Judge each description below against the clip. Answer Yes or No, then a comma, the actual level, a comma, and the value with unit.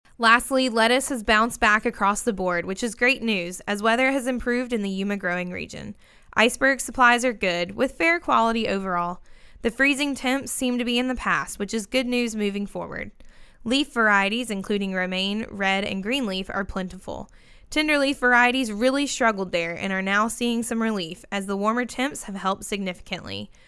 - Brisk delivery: No, average, 180 wpm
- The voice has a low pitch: No, high, 225 Hz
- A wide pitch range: No, average, 4.4 semitones